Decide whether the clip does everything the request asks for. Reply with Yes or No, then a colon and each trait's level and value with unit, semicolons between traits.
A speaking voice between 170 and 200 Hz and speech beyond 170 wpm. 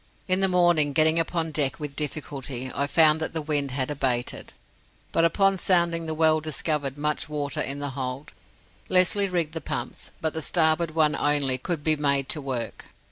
No: medium, 155 Hz; average, 185 wpm